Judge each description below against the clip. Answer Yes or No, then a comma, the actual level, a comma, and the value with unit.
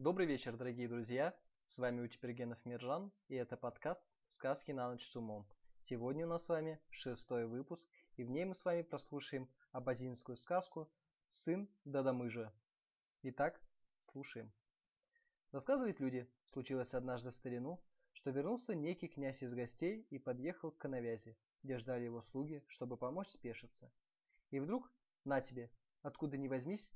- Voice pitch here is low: Yes, low, 130 Hz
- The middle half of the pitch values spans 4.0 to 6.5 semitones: Yes, average, 5.0 semitones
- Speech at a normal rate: Yes, average, 145 wpm